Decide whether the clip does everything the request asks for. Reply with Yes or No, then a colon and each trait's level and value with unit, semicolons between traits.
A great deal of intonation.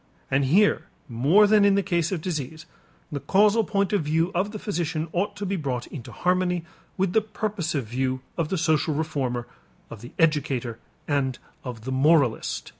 Yes: wide, 6.4 semitones